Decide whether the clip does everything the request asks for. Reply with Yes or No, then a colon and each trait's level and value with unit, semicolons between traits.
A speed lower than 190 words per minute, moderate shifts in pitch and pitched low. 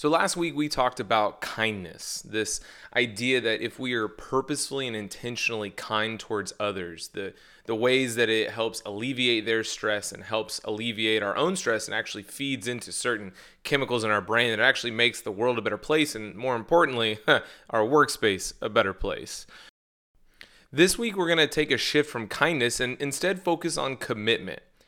Yes: average, 180 wpm; average, 3.8 semitones; low, 120 Hz